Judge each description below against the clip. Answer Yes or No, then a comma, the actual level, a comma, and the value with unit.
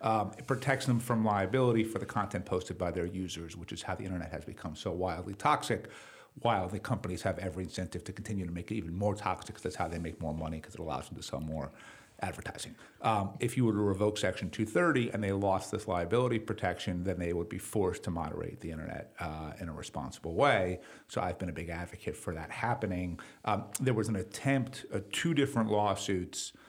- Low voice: Yes, very low, 95 Hz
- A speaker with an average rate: No, fast, 225 wpm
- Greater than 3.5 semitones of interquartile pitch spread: Yes, average, 3.9 semitones